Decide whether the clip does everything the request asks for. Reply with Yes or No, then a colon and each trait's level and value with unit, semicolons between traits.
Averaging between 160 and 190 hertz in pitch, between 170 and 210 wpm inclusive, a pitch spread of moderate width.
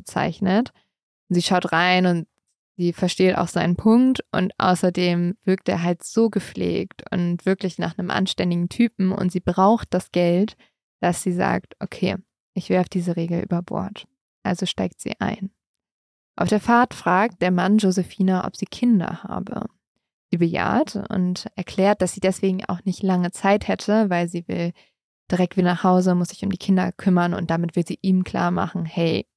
No: medium, 185 Hz; average, 175 wpm; narrow, 1.9 semitones